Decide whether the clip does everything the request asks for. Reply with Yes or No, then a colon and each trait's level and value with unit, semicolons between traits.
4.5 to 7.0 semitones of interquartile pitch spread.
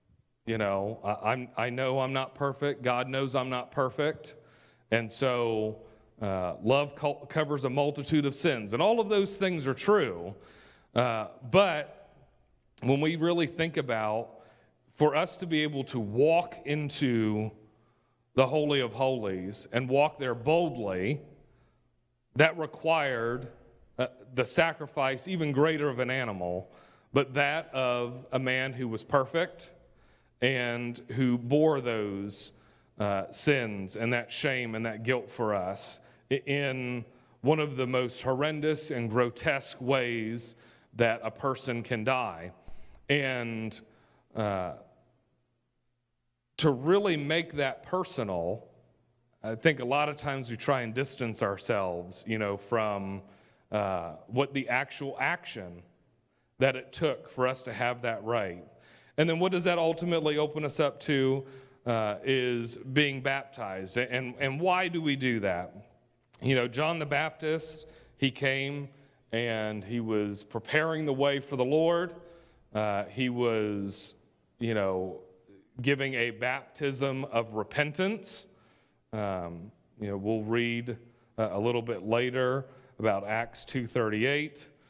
No: average, 4.0 semitones